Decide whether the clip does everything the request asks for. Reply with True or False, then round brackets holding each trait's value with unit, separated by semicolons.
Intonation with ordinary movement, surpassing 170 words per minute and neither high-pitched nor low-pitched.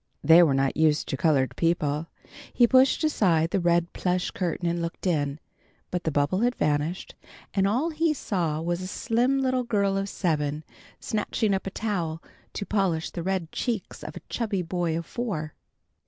True (4.7 semitones; 180 wpm; 180 Hz)